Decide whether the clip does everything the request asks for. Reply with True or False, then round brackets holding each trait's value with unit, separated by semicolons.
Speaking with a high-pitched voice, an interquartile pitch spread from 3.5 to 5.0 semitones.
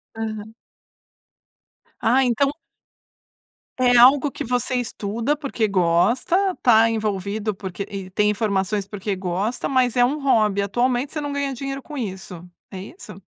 True (225 Hz; 4.5 semitones)